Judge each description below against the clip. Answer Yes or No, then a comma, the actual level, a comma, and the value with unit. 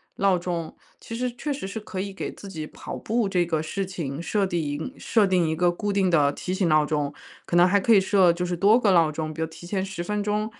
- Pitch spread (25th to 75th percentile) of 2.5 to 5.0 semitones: Yes, average, 3.6 semitones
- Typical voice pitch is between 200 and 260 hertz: No, medium, 185 Hz